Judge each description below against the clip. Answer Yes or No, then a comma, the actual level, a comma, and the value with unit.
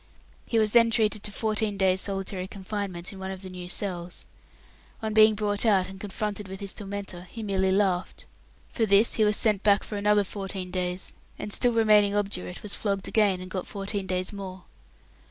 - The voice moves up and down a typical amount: No, narrow, 1.9 semitones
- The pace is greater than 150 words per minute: Yes, average, 190 wpm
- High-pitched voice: Yes, high, 200 Hz